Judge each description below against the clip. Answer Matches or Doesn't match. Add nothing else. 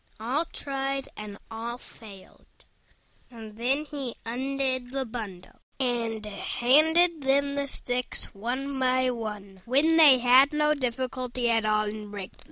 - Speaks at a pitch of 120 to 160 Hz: Doesn't match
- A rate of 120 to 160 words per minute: Matches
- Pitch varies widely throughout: Doesn't match